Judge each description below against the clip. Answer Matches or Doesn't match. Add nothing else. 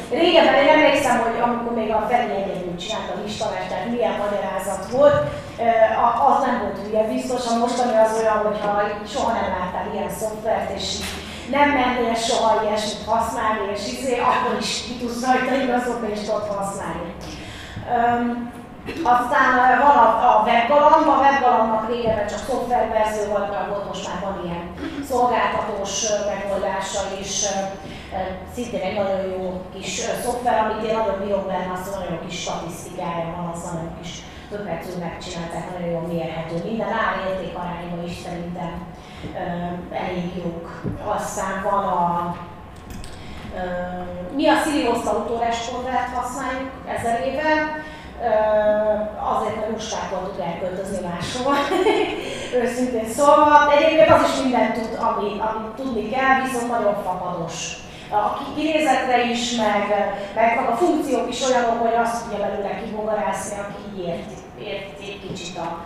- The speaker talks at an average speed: Matches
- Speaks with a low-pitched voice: Doesn't match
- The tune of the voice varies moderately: Matches